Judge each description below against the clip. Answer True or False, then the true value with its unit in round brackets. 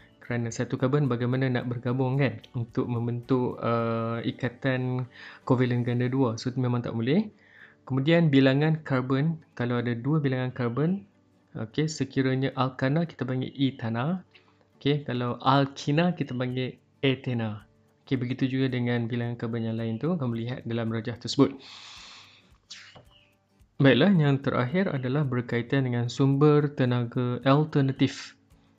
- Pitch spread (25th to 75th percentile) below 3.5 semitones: True (2.4 semitones)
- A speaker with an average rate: True (130 wpm)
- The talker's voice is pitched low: True (125 Hz)